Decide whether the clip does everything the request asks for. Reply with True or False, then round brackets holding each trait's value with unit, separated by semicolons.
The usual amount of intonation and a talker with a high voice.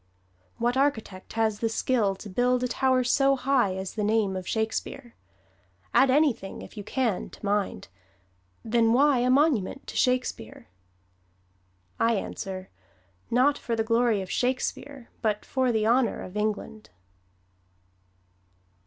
True (3.5 semitones; 230 Hz)